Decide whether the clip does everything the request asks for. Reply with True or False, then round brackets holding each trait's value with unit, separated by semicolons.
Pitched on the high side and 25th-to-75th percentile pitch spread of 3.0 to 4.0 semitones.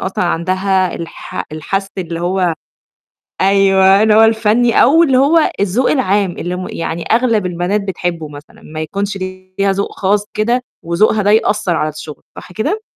True (195 Hz; 3.3 semitones)